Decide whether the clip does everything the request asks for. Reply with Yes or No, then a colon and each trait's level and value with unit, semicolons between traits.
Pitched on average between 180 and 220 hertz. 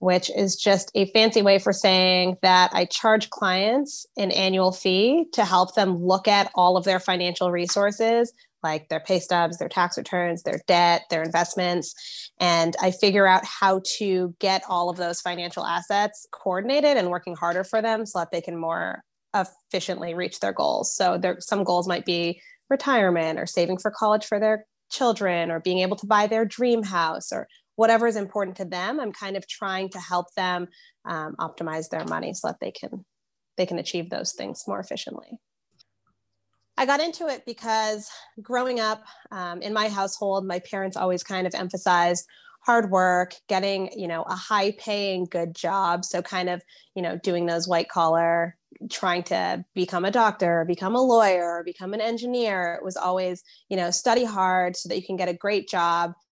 Yes: medium, 185 Hz